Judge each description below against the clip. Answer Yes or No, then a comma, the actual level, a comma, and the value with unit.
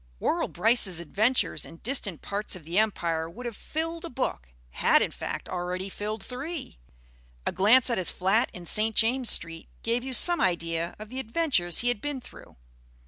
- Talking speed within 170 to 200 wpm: Yes, average, 185 wpm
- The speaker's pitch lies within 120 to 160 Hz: No, high, 215 Hz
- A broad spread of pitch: Yes, wide, 6.1 semitones